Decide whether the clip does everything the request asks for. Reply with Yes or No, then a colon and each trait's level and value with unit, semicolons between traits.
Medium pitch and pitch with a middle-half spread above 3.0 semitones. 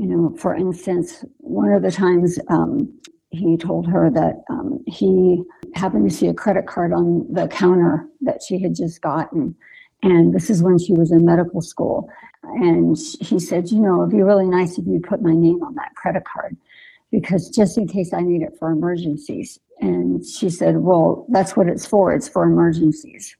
Yes: medium, 180 Hz; average, 3.4 semitones